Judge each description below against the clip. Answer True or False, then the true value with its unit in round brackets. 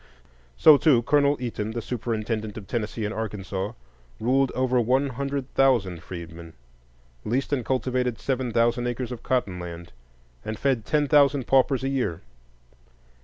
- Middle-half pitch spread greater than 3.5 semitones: True (3.9 semitones)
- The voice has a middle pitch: False (120 Hz)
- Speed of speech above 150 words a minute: False (145 wpm)